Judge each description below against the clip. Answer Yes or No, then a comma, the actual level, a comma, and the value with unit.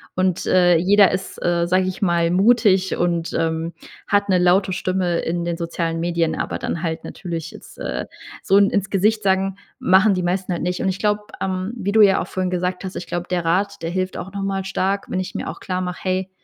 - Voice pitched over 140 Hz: Yes, medium, 185 Hz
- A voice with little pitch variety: Yes, narrow, 1.8 semitones